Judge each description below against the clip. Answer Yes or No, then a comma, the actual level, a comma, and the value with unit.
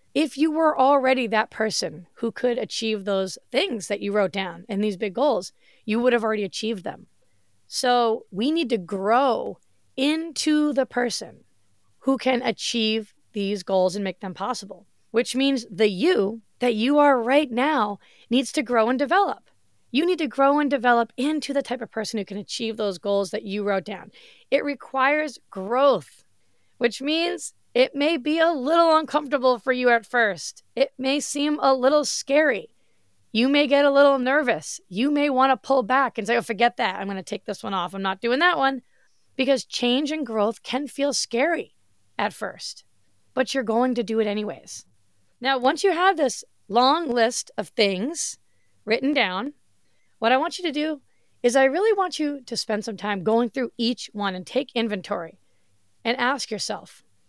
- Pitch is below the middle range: No, high, 245 Hz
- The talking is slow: No, average, 185 wpm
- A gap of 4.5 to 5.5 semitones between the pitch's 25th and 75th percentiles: Yes, average, 4.9 semitones